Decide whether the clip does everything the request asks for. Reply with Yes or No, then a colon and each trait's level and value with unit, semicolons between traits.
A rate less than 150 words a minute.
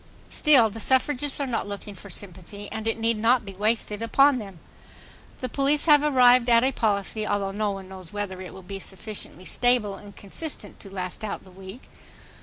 No: average, 195 wpm